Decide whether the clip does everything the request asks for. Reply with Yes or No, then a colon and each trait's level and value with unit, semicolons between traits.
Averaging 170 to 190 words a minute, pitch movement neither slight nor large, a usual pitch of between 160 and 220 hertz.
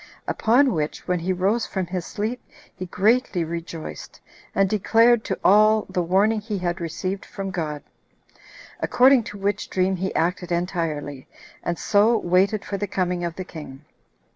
No: average, 160 wpm; average, 3.4 semitones; medium, 185 Hz